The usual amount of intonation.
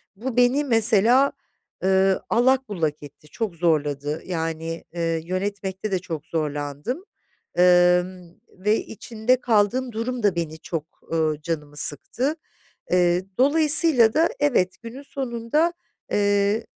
No: wide, 6.6 semitones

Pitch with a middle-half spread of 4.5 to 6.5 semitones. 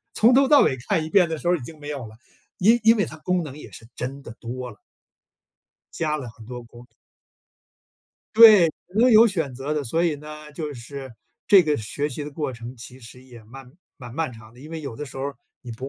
Yes: average, 4.8 semitones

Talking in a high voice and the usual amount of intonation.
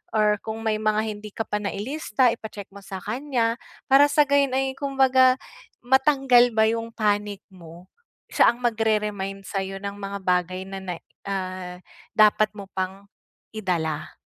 Yes: high, 210 Hz; average, 3.9 semitones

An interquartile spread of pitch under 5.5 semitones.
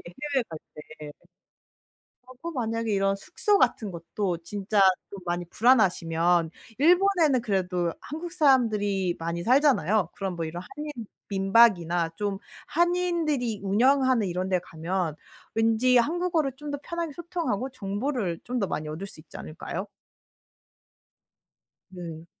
No: wide, 7.6 semitones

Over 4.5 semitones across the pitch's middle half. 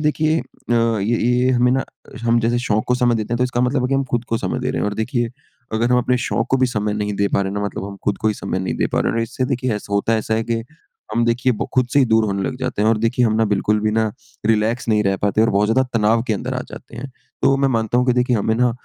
No: narrow, 2.6 semitones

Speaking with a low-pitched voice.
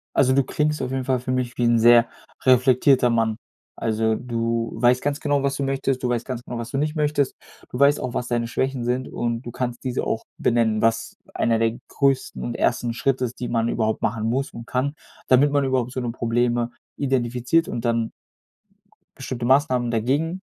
Yes: low, 125 Hz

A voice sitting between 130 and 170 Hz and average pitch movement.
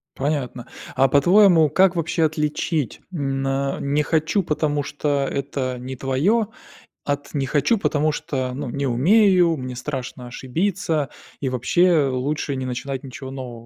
Yes: medium, 140 Hz; average, 3.4 semitones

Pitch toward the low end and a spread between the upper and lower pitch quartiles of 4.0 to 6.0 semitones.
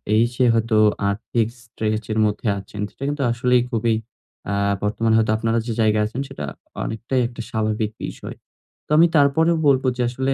No: low, 115 Hz; average, 2.9 semitones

